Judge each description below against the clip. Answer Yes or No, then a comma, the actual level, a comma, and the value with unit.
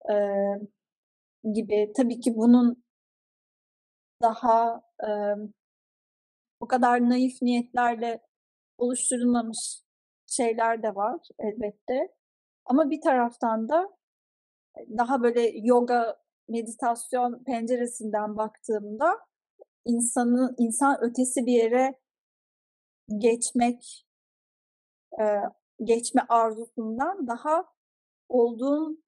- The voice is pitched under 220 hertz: No, high, 240 Hz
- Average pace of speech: No, slow, 75 wpm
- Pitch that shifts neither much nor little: No, narrow, 1.9 semitones